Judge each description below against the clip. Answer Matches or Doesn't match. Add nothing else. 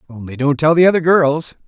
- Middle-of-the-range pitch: Matches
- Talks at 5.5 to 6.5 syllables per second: Matches